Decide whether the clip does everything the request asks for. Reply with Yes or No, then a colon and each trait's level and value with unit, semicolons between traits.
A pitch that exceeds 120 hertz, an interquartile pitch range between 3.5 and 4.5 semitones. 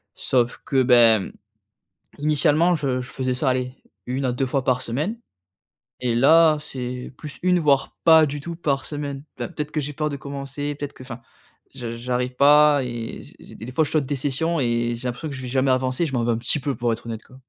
No: low, 135 Hz; average, 2.9 semitones